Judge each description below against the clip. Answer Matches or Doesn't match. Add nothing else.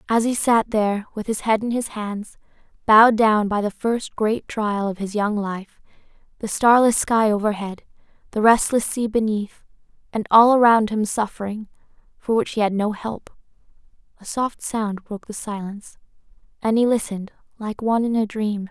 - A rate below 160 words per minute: Doesn't match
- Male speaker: Doesn't match